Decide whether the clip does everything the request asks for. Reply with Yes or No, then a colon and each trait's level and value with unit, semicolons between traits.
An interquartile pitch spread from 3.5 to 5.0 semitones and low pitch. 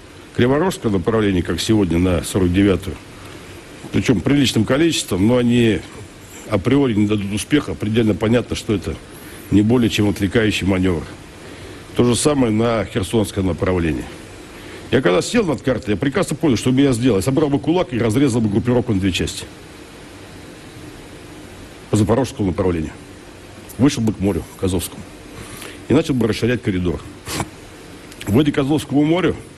Yes: average, 4.2 semitones; low, 105 Hz